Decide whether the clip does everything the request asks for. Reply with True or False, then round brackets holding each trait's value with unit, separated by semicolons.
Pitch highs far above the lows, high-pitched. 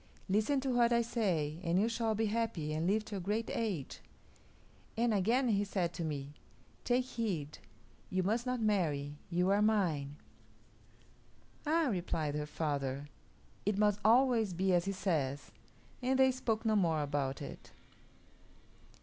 True (6.4 semitones; 195 Hz)